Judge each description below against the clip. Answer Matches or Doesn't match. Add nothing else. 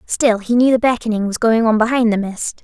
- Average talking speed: Doesn't match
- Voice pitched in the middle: Doesn't match